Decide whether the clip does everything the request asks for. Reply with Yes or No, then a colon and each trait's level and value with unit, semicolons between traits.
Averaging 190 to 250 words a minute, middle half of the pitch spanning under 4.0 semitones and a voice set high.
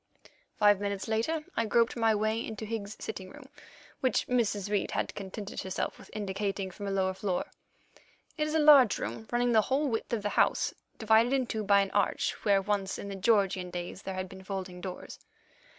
Yes: average, 200 wpm; average, 3.0 semitones; high, 205 Hz